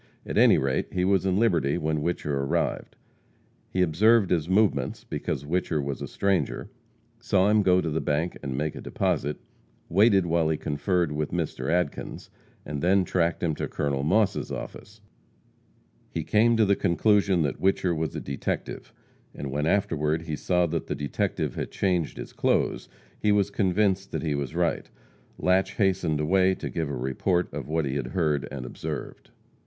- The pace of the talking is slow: No, average, 175 wpm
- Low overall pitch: Yes, very low, 85 Hz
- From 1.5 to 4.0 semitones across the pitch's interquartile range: No, average, 4.4 semitones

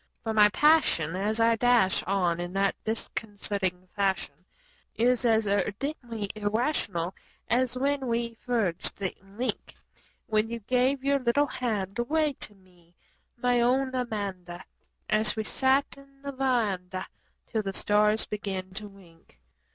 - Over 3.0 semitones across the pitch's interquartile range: Yes, average, 4.3 semitones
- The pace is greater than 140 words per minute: No, slow, 135 wpm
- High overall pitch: Yes, high, 220 Hz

